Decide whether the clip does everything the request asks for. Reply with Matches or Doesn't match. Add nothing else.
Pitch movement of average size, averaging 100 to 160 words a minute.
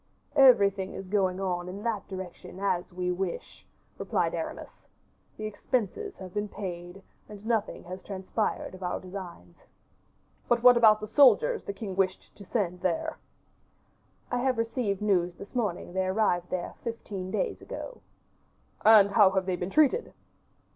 Matches